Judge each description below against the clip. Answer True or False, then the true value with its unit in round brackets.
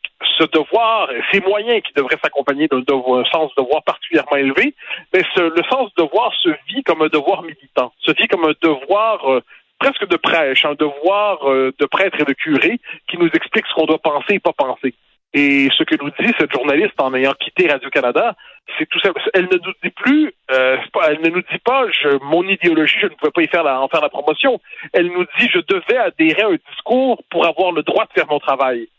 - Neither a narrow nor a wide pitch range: False (6.0 semitones)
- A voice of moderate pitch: True (160 Hz)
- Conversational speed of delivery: False (225 wpm)